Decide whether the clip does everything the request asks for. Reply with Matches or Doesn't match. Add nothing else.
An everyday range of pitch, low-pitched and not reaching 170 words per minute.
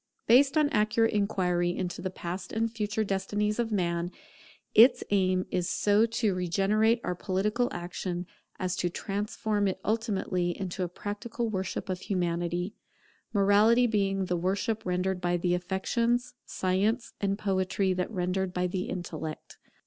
Doesn't match